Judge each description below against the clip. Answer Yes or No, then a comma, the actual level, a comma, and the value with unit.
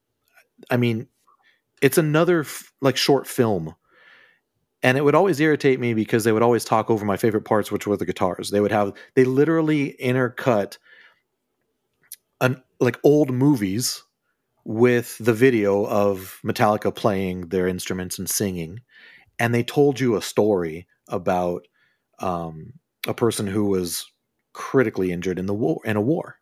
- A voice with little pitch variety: No, average, 4.5 semitones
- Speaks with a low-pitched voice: Yes, low, 115 Hz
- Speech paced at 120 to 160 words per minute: Yes, average, 150 wpm